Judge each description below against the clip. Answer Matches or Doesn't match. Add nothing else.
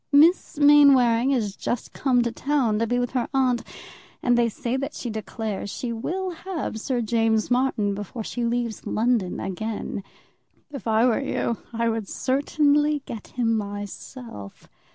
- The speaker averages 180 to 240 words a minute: Doesn't match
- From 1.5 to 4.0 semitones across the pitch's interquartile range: Matches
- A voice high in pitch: Matches